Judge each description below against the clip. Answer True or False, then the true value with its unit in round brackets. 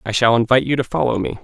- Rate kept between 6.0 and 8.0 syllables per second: True (7.5 syllables/s)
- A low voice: True (120 Hz)